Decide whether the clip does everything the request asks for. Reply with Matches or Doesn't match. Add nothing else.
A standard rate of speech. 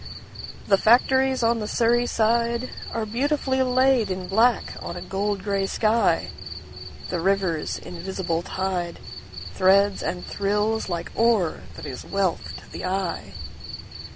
Doesn't match